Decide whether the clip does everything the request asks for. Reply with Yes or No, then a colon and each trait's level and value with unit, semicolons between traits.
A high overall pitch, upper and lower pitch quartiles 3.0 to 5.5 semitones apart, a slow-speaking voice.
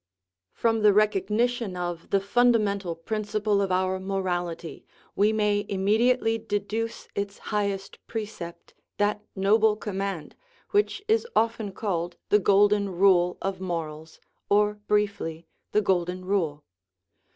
No: high, 200 Hz; narrow, 2.5 semitones; slow, 120 wpm